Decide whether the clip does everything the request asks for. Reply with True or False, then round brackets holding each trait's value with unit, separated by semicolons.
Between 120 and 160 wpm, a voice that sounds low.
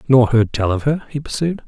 False (250 wpm; 130 Hz)